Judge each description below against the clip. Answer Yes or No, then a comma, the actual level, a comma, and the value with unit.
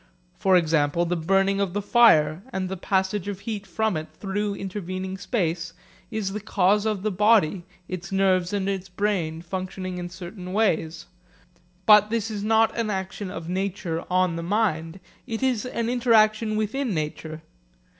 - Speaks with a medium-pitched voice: No, high, 195 Hz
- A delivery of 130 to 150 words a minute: No, average, 165 wpm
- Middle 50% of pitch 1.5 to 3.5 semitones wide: Yes, average, 3.2 semitones